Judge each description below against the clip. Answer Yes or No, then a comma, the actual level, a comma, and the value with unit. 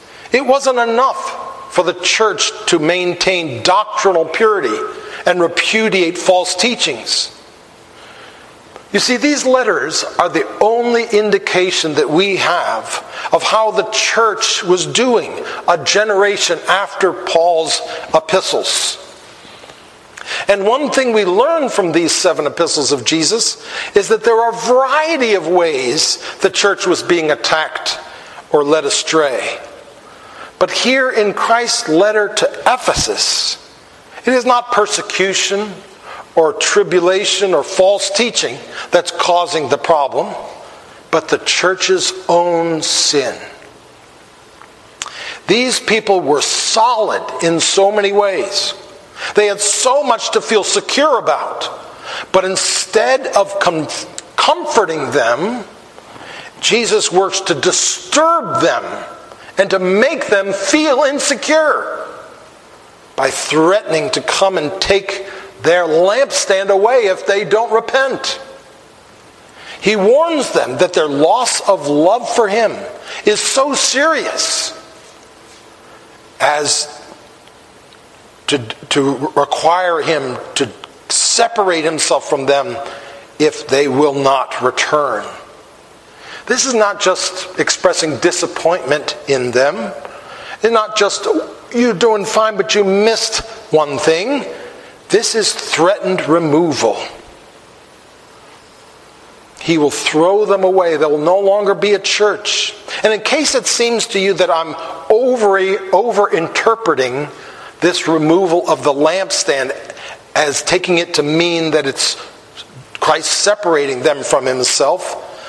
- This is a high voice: Yes, high, 200 Hz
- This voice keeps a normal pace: No, slow, 115 wpm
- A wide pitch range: No, average, 5.0 semitones